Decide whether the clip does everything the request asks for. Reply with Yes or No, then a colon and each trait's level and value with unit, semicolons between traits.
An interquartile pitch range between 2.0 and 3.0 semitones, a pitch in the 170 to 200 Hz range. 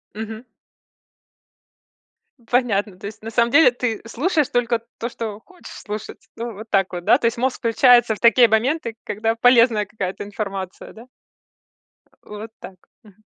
No: narrow, 2.5 semitones; high, 225 Hz